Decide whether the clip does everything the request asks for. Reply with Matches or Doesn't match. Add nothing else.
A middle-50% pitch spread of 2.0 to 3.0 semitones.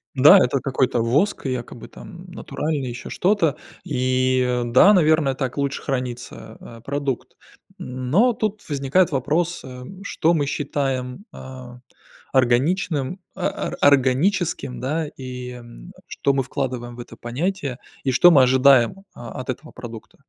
Doesn't match